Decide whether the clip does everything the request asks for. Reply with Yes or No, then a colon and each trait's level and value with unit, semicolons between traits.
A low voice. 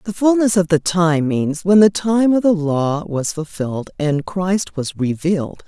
No: medium, 175 Hz